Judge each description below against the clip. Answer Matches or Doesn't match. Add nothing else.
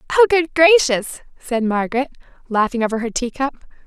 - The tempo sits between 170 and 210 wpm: Doesn't match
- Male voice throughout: Doesn't match